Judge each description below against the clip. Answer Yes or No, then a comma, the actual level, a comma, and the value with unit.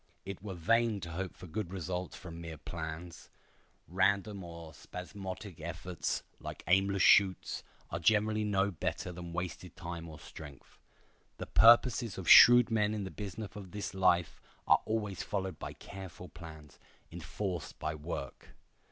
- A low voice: Yes, very low, 95 Hz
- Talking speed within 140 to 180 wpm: Yes, average, 150 wpm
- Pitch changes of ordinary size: Yes, average, 3.3 semitones